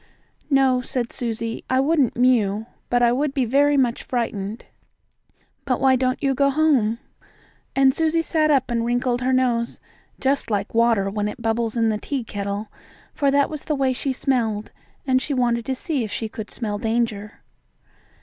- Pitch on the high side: Yes, high, 245 Hz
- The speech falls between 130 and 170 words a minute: No, average, 180 wpm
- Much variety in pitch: No, average, 3.2 semitones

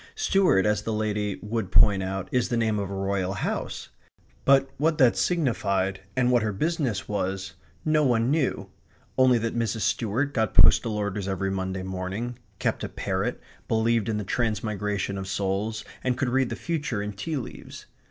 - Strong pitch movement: No, average, 4.2 semitones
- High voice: No, low, 110 Hz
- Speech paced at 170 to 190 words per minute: Yes, average, 175 wpm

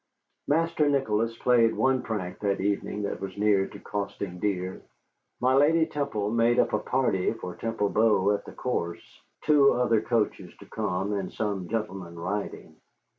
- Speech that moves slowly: No, average, 160 wpm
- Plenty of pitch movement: No, average, 4.1 semitones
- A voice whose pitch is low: Yes, low, 105 Hz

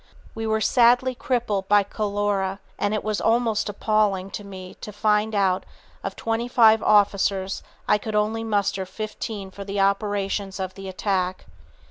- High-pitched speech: Yes, high, 205 Hz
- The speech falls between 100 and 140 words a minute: No, average, 160 wpm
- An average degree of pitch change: No, narrow, 1.9 semitones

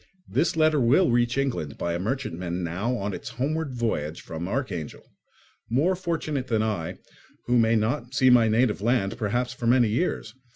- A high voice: No, low, 120 Hz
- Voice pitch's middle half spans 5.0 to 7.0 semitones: No, average, 4.5 semitones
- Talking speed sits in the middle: Yes, average, 170 wpm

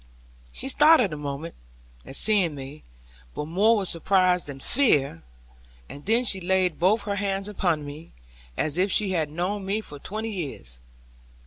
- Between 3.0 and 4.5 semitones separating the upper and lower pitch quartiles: No, wide, 5.4 semitones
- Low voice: No, medium, 185 Hz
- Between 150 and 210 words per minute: Yes, average, 160 wpm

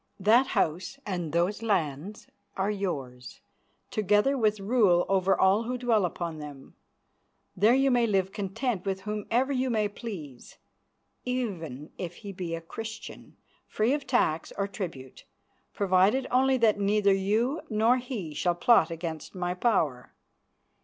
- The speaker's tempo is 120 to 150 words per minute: Yes, average, 140 wpm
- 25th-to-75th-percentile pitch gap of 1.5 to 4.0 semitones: No, average, 4.9 semitones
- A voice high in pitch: Yes, high, 200 Hz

